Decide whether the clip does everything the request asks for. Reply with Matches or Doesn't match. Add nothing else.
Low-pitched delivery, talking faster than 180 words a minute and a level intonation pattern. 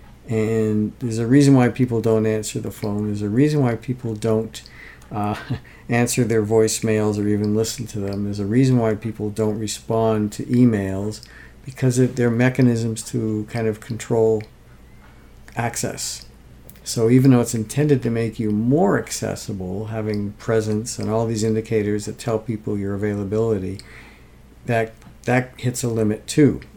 Doesn't match